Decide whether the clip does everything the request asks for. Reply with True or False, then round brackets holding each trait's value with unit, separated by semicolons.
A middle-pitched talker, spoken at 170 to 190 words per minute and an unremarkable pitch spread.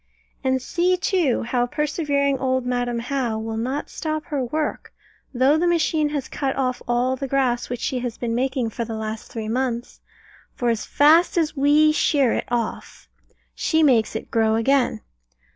False (260 Hz; 175 wpm; 3.6 semitones)